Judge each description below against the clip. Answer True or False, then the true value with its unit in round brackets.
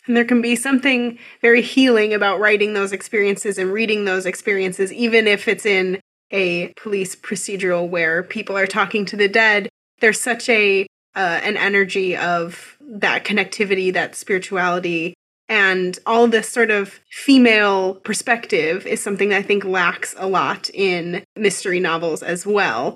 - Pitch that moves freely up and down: False (3.1 semitones)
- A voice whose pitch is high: True (200 Hz)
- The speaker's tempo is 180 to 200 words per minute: False (155 wpm)